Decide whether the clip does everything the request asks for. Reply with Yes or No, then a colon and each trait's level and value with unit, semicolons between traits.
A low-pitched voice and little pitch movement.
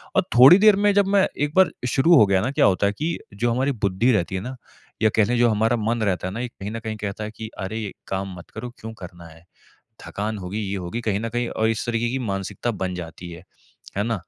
No: low, 110 Hz; average, 3.9 semitones